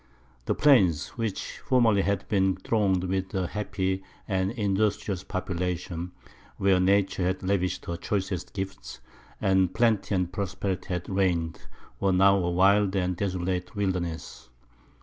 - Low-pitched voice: Yes, very low, 95 Hz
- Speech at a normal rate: No, slow, 130 wpm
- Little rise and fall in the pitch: Yes, narrow, 1.7 semitones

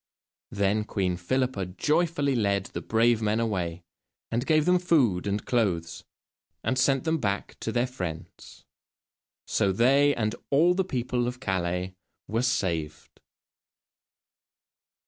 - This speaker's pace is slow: Yes, slow, 125 wpm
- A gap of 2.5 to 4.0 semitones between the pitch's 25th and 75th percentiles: No, wide, 5.6 semitones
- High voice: No, low, 115 Hz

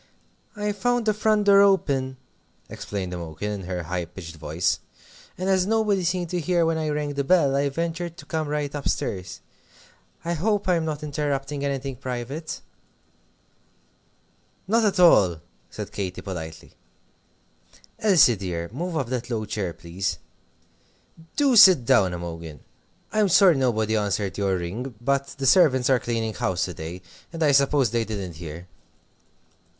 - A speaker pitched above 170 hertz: No, low, 135 Hz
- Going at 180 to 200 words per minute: No, average, 155 wpm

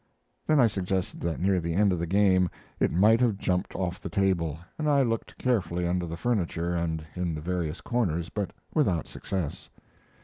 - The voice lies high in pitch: No, very low, 90 Hz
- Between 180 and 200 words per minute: Yes, average, 190 wpm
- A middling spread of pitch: Yes, average, 3.4 semitones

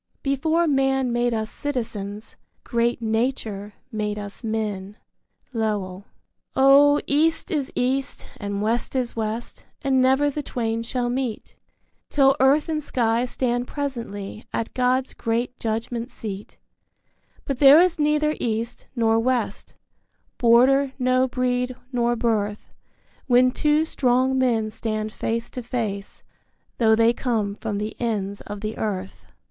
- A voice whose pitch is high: Yes, high, 240 Hz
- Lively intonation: No, average, 3.4 semitones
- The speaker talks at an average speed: No, slow, 130 wpm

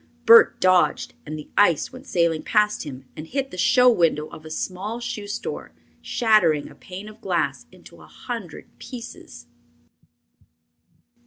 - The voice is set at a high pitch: Yes, high, 195 Hz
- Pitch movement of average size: No, wide, 6.2 semitones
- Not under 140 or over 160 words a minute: Yes, average, 150 wpm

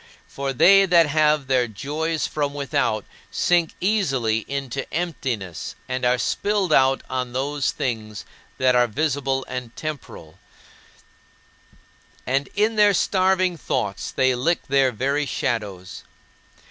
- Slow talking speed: Yes, slow, 120 wpm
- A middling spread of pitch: Yes, average, 4.5 semitones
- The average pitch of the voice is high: No, low, 135 Hz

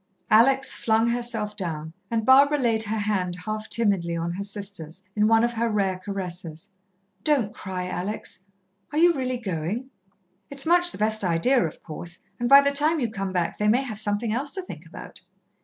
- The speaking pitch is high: Yes, high, 215 Hz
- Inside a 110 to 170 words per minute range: No, average, 190 wpm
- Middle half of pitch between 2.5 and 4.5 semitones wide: No, average, 4.9 semitones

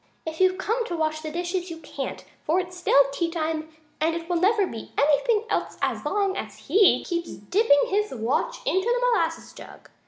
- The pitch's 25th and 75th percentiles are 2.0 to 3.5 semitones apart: No, average, 4.0 semitones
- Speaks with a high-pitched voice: Yes, very high, 345 Hz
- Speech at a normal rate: Yes, average, 195 wpm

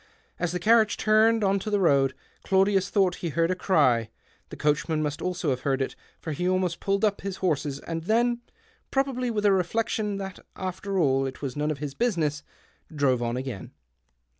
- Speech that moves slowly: No, average, 200 wpm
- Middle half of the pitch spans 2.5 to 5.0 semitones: No, wide, 5.6 semitones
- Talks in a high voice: No, medium, 180 Hz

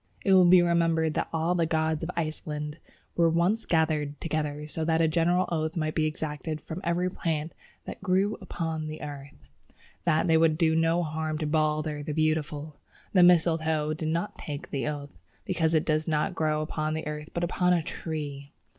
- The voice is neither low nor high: Yes, medium, 160 Hz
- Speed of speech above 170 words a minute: Yes, average, 190 wpm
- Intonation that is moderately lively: No, narrow, 1.6 semitones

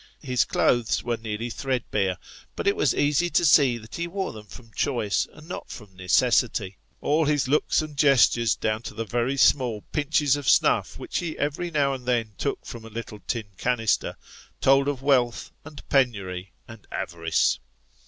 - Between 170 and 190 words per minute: Yes, average, 175 wpm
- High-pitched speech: No, low, 125 Hz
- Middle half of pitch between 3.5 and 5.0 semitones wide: Yes, average, 4.7 semitones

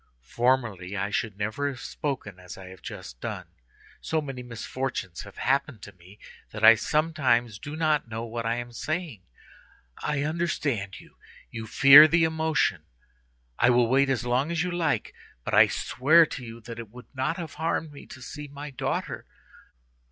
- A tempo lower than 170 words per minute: No, average, 175 wpm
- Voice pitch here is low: Yes, low, 125 Hz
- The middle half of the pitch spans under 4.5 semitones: No, average, 5.2 semitones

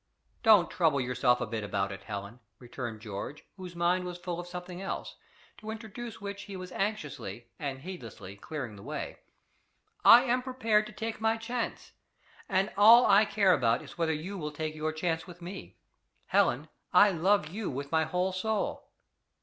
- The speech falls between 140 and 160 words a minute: No, average, 175 wpm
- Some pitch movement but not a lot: No, wide, 7.3 semitones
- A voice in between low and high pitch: Yes, medium, 175 Hz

